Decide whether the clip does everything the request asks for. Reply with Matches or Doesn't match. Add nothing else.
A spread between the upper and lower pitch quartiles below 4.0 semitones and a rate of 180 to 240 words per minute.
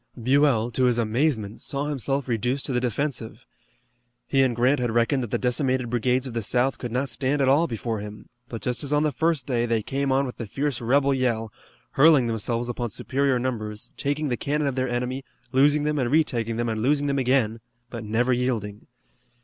Matches